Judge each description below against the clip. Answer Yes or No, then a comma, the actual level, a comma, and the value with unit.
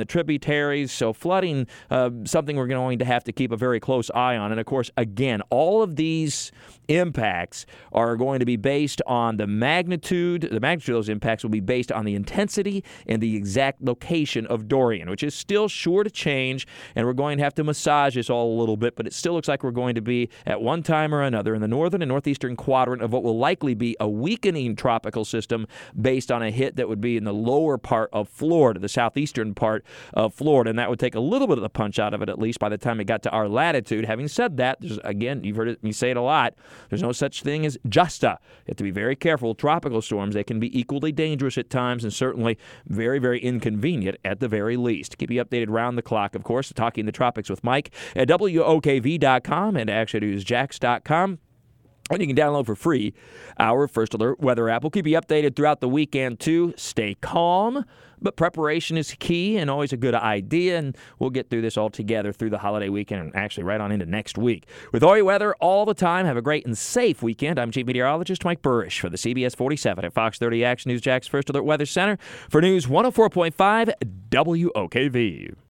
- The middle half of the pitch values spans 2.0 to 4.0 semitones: No, average, 4.9 semitones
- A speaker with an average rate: No, fast, 225 wpm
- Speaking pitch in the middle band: No, low, 125 Hz